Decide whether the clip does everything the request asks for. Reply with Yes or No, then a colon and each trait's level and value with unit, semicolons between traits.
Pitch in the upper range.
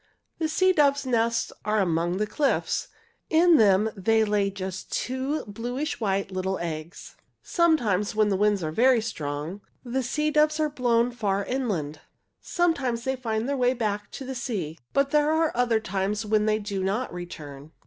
Yes: high, 220 Hz